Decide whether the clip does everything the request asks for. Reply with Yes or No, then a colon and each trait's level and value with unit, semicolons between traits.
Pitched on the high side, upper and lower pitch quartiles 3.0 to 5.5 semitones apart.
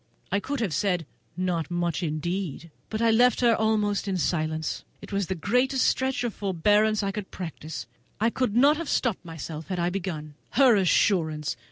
Yes: high, 195 Hz; average, 4.9 semitones